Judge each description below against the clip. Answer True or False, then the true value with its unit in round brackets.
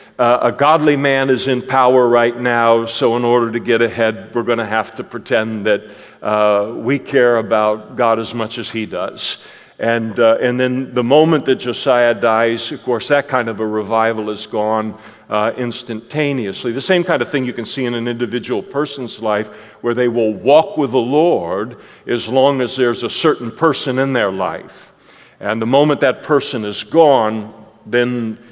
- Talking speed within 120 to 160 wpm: False (195 wpm)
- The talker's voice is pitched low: True (120 Hz)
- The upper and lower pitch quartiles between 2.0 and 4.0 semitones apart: True (2.6 semitones)